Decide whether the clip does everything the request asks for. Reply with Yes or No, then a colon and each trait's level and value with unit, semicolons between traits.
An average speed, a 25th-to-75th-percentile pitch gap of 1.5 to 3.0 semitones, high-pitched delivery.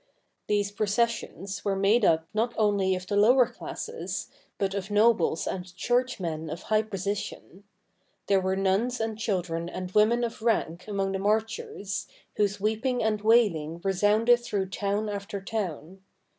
Yes: average, 145 wpm; average, 2.7 semitones; high, 205 Hz